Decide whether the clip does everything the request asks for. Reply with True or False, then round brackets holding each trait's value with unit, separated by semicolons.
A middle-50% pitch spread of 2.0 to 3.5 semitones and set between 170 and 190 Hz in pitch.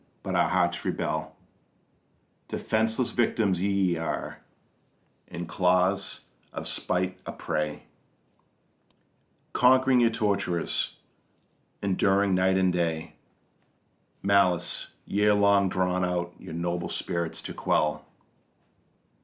False (2.7 semitones; 95 Hz)